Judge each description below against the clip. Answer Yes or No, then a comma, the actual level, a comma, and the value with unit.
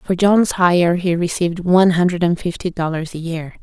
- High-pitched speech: No, medium, 175 Hz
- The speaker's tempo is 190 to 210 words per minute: Yes, average, 200 wpm